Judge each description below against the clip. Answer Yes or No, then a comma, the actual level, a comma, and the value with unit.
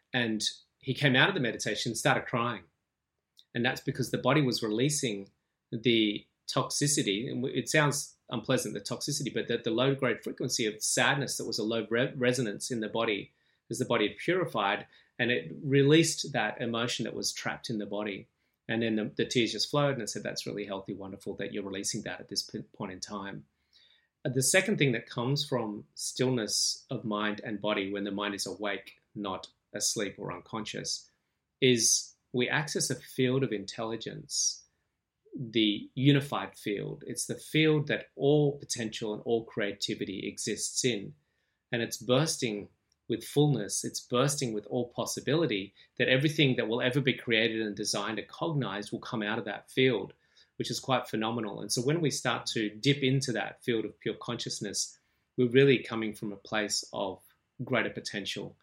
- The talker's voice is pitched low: Yes, low, 120 Hz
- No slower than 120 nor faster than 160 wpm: No, average, 180 wpm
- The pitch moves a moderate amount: Yes, average, 4.1 semitones